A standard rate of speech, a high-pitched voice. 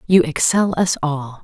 No: average, 165 wpm; medium, 160 Hz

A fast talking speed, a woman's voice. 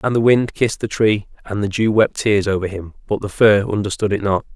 No: fast, 250 wpm; male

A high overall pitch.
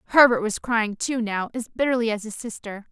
Yes: high, 225 Hz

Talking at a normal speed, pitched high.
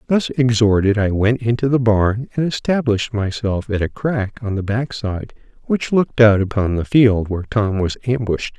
No: average, 190 wpm; low, 110 Hz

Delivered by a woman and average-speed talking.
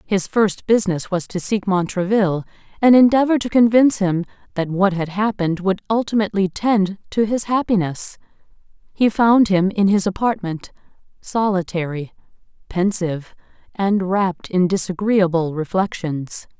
No: female; slow, 125 wpm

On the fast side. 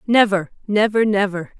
No: slow, 115 wpm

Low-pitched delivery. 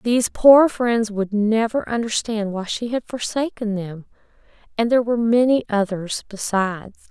No: high, 220 Hz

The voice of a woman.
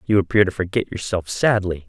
No: male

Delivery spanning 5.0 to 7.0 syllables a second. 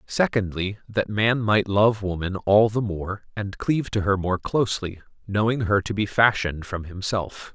No: 4.6 syllables/s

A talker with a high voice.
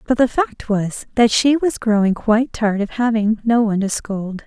Yes: high, 225 Hz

